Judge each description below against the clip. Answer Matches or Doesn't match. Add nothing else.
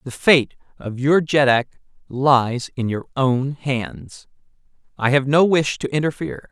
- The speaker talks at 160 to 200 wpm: Doesn't match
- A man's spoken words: Matches